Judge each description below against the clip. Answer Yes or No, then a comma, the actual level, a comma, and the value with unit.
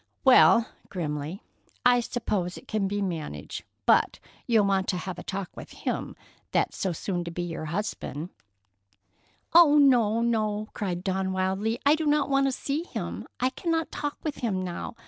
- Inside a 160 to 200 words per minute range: Yes, average, 165 wpm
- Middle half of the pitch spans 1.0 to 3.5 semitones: No, wide, 5.6 semitones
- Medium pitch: No, high, 205 Hz